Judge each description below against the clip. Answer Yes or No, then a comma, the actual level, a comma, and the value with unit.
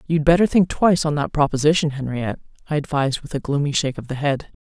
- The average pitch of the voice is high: No, medium, 150 Hz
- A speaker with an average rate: No, fast, 220 wpm